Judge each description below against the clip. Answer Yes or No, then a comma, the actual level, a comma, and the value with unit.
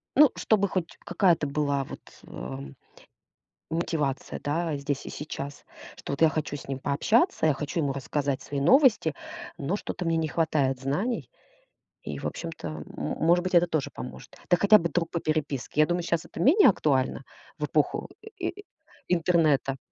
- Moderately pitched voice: Yes, medium, 155 Hz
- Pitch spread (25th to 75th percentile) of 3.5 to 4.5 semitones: Yes, average, 3.9 semitones